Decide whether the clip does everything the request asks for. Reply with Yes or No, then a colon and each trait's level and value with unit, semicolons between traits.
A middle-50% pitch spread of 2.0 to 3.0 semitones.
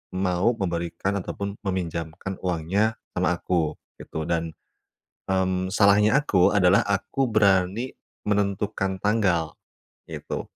Yes: narrow, 2.6 semitones